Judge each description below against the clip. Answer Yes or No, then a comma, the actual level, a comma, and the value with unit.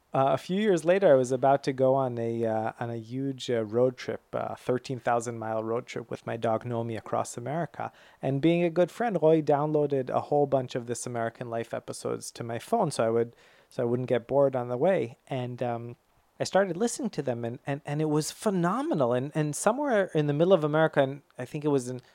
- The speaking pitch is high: No, low, 135 Hz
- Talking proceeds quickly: Yes, fast, 240 wpm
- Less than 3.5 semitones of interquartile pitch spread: No, average, 4.2 semitones